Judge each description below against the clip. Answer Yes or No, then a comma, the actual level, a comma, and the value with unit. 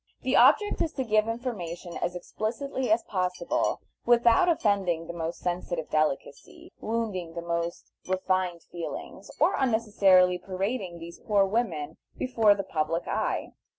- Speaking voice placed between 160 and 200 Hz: Yes, medium, 185 Hz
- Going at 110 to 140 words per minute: Yes, slow, 135 wpm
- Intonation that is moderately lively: Yes, average, 4.8 semitones